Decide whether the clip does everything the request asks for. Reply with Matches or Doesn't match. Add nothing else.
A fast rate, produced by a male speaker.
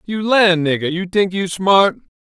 Doesn't match